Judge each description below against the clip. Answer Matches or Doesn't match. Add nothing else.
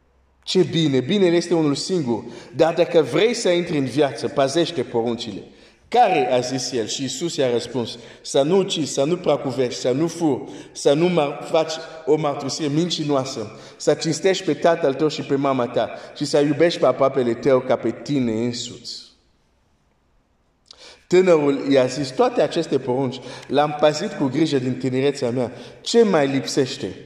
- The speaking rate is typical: Matches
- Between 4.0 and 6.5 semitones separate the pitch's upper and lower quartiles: Matches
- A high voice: Doesn't match